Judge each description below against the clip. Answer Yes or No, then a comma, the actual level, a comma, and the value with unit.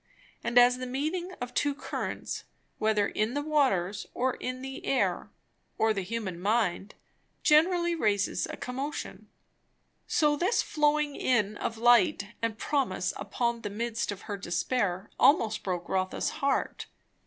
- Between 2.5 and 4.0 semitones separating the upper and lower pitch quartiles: No, wide, 5.5 semitones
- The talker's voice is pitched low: No, high, 235 Hz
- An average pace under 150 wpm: Yes, average, 140 wpm